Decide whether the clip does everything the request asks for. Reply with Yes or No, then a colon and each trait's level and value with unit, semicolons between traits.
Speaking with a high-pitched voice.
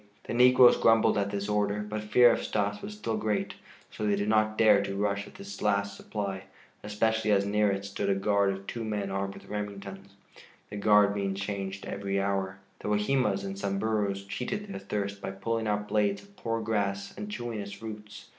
No: low, 105 Hz